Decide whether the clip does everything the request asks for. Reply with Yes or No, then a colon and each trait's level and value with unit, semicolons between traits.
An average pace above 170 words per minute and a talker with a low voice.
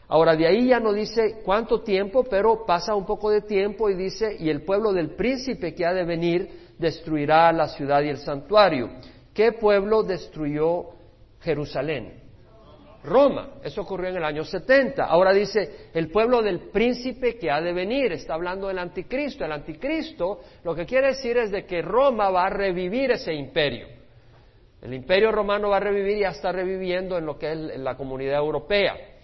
No: average, 180 wpm; high, 190 Hz